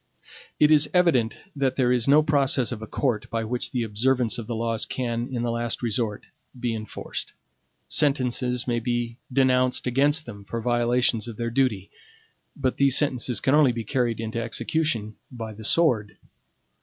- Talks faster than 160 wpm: Yes, average, 170 wpm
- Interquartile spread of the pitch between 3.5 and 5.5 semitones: No, narrow, 2.5 semitones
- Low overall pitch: Yes, low, 120 Hz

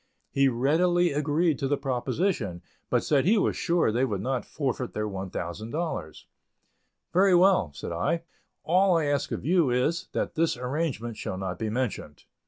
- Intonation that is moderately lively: No, wide, 7.3 semitones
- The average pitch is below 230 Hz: Yes, low, 135 Hz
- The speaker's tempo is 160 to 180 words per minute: Yes, average, 165 wpm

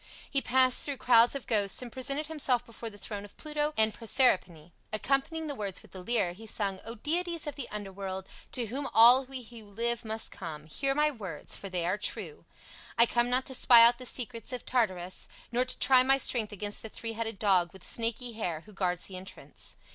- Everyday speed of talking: No, fast, 215 wpm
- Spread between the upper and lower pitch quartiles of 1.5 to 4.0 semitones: No, average, 4.4 semitones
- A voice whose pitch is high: Yes, high, 230 Hz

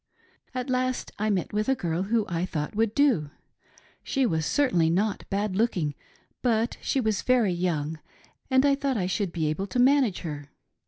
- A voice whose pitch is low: No, high, 210 Hz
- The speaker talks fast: No, average, 180 wpm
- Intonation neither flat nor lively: No, wide, 6.7 semitones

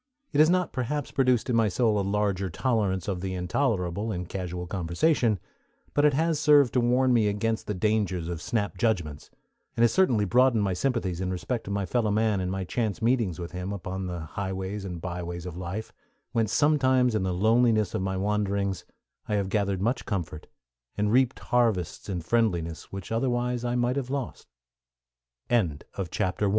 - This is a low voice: Yes, low, 105 Hz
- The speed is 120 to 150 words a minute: No, average, 170 wpm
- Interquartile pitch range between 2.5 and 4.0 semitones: No, average, 4.6 semitones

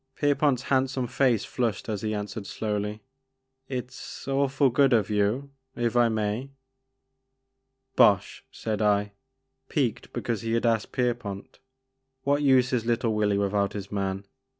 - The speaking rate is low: No, average, 155 wpm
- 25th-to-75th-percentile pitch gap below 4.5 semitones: Yes, average, 4.0 semitones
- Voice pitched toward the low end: Yes, low, 120 Hz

